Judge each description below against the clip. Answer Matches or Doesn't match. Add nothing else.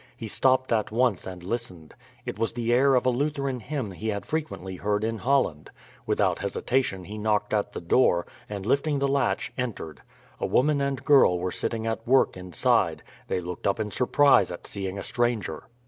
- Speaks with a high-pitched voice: Doesn't match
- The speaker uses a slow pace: Doesn't match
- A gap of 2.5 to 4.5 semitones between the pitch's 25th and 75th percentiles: Doesn't match